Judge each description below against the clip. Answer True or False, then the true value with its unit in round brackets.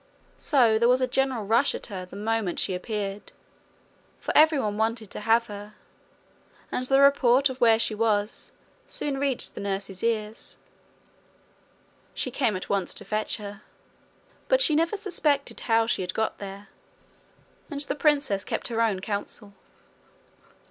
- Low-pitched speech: False (225 Hz)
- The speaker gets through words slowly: False (155 wpm)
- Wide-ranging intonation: False (4.6 semitones)